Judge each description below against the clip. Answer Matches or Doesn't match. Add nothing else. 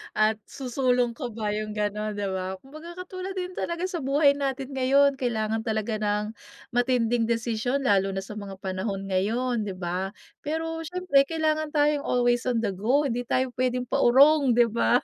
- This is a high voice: Matches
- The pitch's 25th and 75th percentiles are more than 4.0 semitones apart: Matches